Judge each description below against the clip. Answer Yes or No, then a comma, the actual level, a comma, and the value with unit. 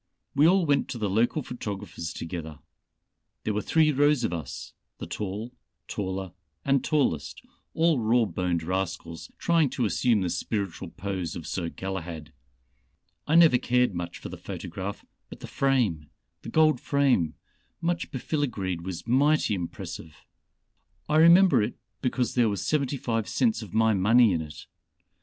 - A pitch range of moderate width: No, wide, 7.4 semitones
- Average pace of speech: Yes, average, 150 wpm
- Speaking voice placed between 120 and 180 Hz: No, low, 110 Hz